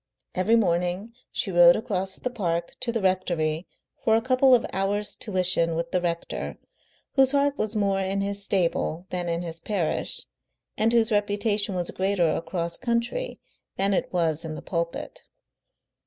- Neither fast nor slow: Yes, average, 160 wpm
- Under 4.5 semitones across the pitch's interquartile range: Yes, average, 4.1 semitones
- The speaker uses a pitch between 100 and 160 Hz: No, high, 190 Hz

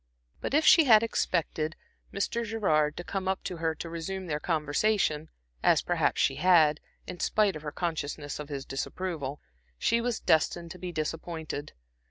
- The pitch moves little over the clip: No, average, 4.0 semitones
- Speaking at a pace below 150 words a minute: No, average, 170 wpm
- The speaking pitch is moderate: Yes, medium, 165 Hz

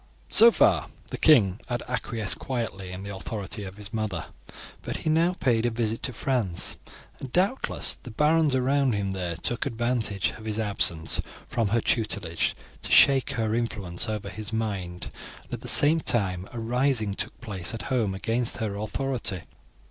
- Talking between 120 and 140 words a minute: No, average, 170 wpm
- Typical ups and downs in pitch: Yes, average, 4.1 semitones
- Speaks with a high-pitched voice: No, low, 110 Hz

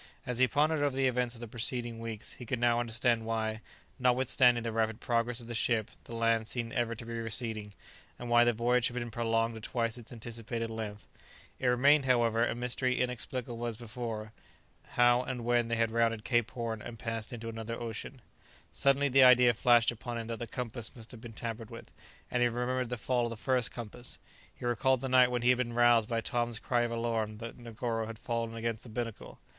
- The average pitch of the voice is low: Yes, low, 120 Hz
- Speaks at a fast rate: Yes, fast, 215 wpm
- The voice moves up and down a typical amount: No, narrow, 1.3 semitones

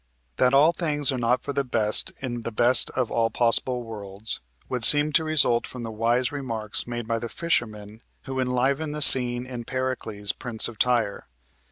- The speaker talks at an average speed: Yes, average, 185 wpm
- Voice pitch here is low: Yes, low, 120 Hz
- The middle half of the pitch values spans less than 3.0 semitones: Yes, narrow, 2.6 semitones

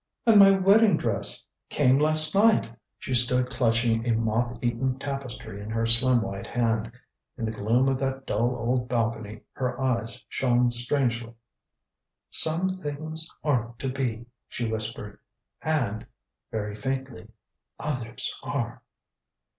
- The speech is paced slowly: Yes, slow, 130 wpm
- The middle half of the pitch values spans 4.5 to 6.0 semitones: No, average, 3.0 semitones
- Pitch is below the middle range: Yes, low, 120 Hz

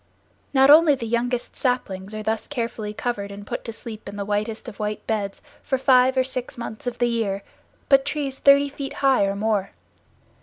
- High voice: Yes, high, 235 Hz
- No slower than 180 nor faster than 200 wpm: Yes, average, 195 wpm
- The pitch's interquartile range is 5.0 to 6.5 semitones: No, average, 4.1 semitones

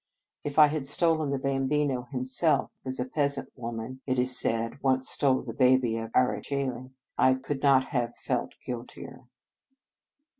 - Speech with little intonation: Yes, narrow, 1.9 semitones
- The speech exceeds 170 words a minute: No, average, 160 wpm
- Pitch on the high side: No, low, 130 Hz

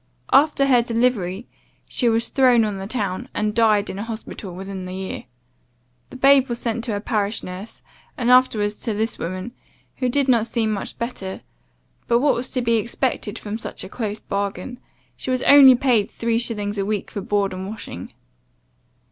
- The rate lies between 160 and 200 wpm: Yes, average, 185 wpm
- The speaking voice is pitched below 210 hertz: No, high, 225 Hz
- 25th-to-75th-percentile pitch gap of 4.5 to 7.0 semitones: No, average, 3.5 semitones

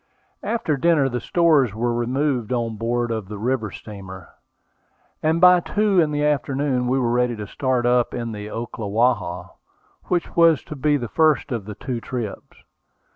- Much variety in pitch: No, average, 4.5 semitones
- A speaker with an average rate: Yes, average, 165 wpm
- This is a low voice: Yes, low, 125 Hz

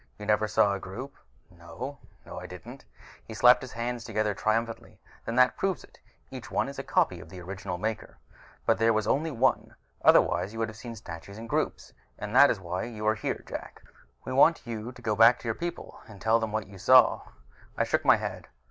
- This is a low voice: Yes, low, 110 Hz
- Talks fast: Yes, fast, 215 wpm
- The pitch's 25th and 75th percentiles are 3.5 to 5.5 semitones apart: No, average, 3.1 semitones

